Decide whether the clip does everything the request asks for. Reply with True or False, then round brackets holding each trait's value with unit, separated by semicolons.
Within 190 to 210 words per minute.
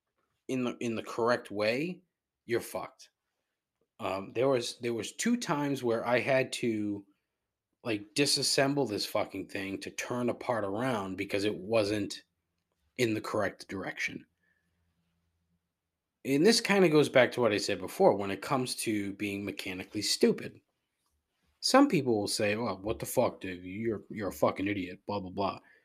False (165 wpm)